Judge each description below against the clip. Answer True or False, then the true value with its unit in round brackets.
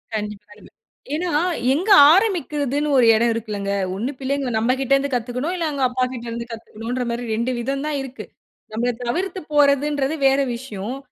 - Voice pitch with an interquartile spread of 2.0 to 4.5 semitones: True (3.4 semitones)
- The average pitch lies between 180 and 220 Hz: False (255 Hz)